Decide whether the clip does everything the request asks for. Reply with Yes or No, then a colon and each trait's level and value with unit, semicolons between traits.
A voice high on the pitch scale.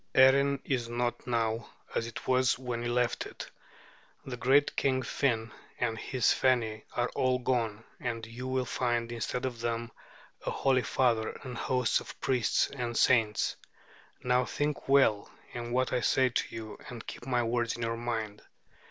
No: low, 120 Hz